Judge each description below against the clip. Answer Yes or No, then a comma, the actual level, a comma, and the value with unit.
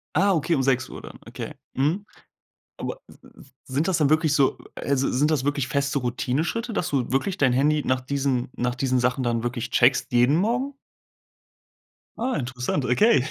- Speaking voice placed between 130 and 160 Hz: Yes, medium, 140 Hz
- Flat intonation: No, average, 3.7 semitones